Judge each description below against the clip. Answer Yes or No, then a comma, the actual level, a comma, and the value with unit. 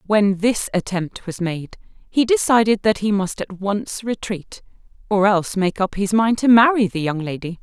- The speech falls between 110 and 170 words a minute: No, average, 180 wpm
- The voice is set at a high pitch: Yes, high, 200 Hz